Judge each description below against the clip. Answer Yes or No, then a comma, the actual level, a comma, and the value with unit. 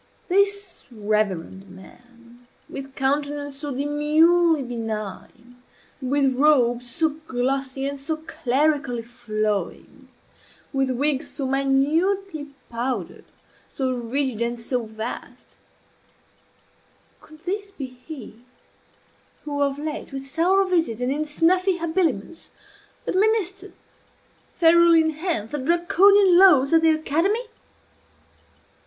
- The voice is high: Yes, very high, 280 Hz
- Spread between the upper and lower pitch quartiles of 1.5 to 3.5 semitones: No, average, 5.1 semitones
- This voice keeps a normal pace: No, slow, 105 wpm